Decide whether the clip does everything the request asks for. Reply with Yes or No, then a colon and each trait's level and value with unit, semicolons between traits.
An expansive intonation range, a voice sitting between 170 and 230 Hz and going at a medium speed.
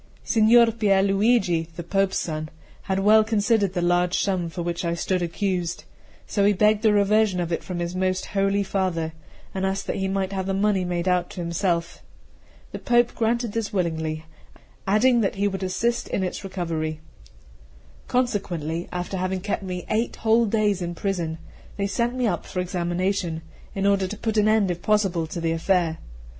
No: average, 3.1 semitones; high, 190 Hz; average, 185 wpm